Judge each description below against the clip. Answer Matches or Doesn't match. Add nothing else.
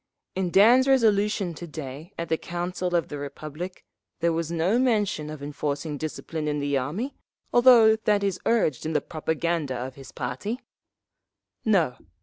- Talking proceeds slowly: Doesn't match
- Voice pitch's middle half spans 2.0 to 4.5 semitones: Doesn't match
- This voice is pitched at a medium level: Matches